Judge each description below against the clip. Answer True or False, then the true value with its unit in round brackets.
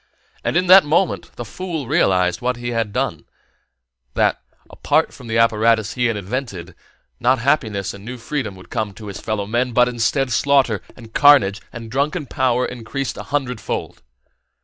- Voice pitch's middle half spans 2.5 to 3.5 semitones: False (4.0 semitones)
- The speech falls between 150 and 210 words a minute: True (165 wpm)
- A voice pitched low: True (120 Hz)